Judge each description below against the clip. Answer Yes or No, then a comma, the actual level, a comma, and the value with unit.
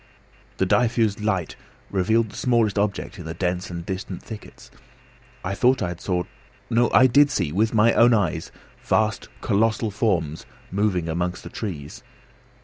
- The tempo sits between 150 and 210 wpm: Yes, average, 155 wpm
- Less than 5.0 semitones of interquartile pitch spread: Yes, average, 4.1 semitones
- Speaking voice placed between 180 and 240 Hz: No, low, 100 Hz